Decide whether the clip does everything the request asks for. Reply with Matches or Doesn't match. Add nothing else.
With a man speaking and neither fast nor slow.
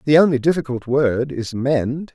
Matches